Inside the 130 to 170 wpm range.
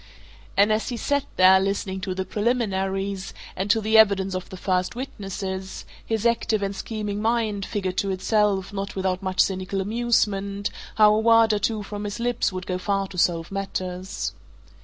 No: average, 180 wpm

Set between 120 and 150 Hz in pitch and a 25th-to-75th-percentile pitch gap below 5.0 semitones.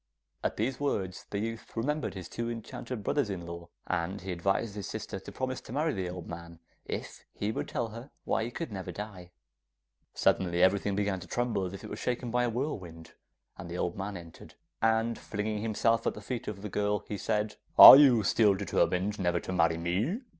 No: low, 105 Hz; average, 4.0 semitones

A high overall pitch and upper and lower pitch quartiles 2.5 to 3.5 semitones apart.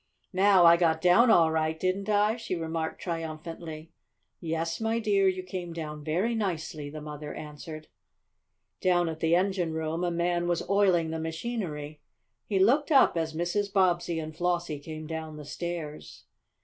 No: medium, 170 Hz; average, 2.8 semitones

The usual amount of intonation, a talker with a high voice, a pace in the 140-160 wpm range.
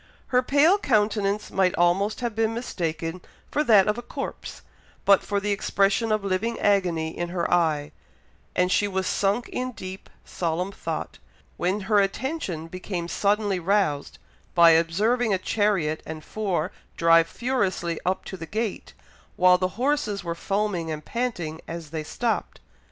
Yes: average, 4.0 semitones; high, 195 Hz; average, 155 wpm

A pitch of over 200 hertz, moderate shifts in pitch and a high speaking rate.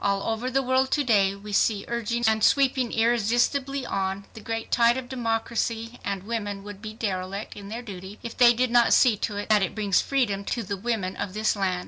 Yes: high, 225 Hz; average, 3.2 semitones; fast, 215 wpm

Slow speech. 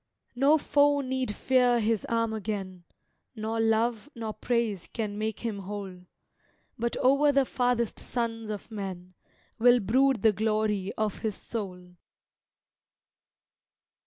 Yes: slow, 125 wpm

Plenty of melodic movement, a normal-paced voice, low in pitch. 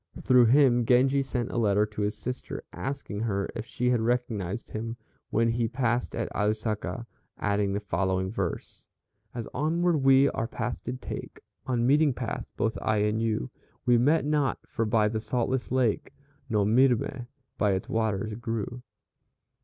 No: average, 3.1 semitones; average, 160 wpm; low, 115 Hz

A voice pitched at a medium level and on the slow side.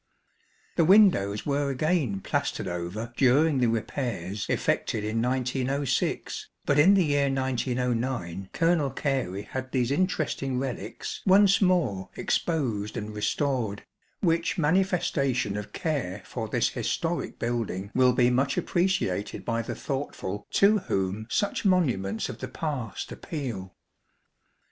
No: low, 130 Hz; slow, 125 wpm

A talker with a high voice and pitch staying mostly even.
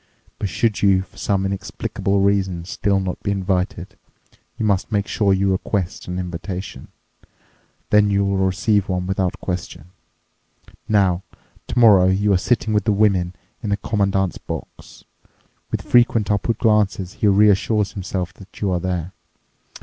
No: very low, 95 Hz; narrow, 1.9 semitones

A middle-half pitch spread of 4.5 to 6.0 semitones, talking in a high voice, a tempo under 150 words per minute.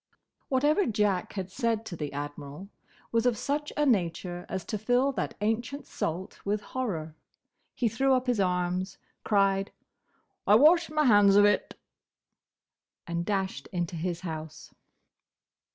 Yes: wide, 5.6 semitones; high, 200 Hz; average, 140 wpm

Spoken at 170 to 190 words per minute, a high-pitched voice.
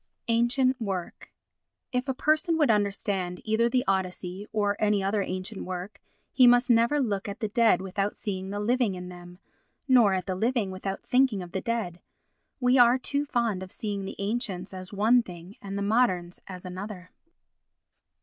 Yes: average, 175 wpm; high, 205 Hz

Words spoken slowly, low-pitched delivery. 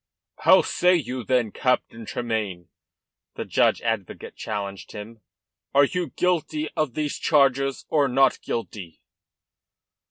Yes: slow, 120 wpm; low, 125 Hz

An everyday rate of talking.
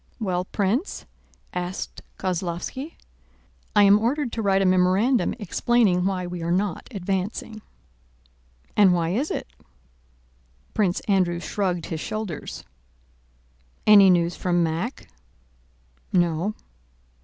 No: slow, 110 wpm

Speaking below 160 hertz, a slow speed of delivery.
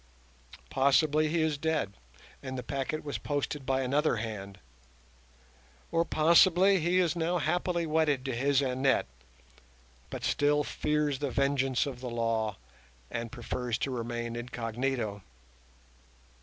Yes: low, 135 Hz; slow, 130 wpm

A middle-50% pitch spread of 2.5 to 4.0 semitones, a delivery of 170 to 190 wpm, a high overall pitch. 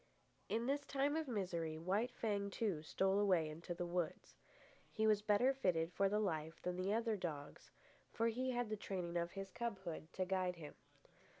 No: average, 4.4 semitones; average, 185 wpm; high, 195 Hz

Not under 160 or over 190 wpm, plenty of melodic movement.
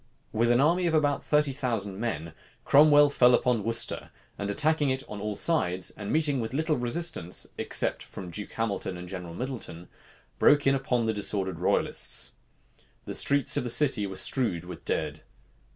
Yes: average, 170 wpm; wide, 6.4 semitones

